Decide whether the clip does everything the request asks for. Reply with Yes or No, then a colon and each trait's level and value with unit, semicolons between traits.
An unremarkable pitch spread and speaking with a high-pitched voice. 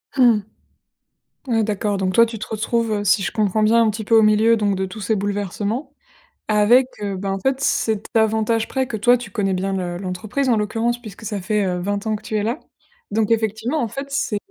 No: narrow, 2.2 semitones; high, 215 Hz